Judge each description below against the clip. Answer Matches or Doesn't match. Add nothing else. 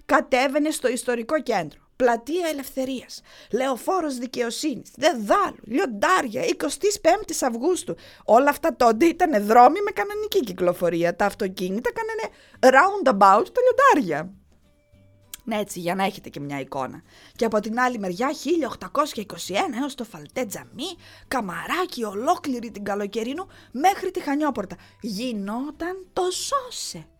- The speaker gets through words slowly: Matches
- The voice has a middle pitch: Doesn't match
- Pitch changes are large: Matches